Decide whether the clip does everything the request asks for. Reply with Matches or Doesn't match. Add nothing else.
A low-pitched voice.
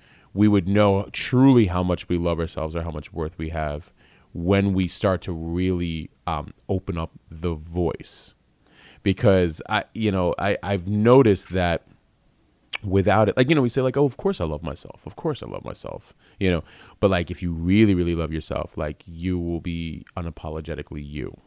Matches